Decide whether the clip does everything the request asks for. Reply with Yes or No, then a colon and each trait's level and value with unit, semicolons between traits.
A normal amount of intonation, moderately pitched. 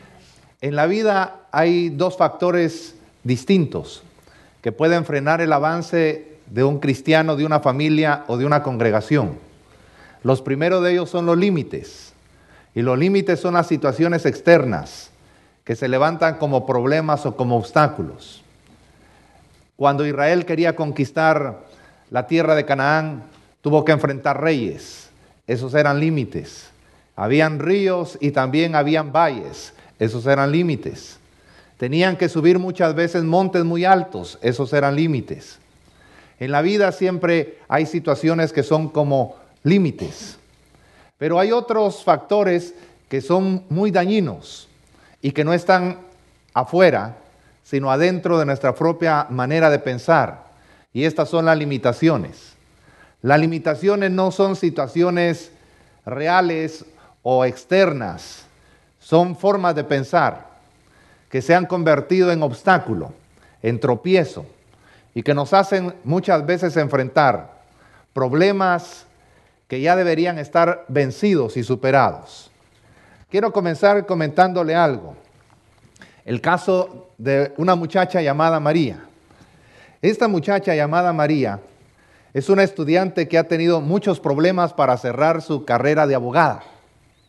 Yes: average, 4.2 semitones; medium, 160 Hz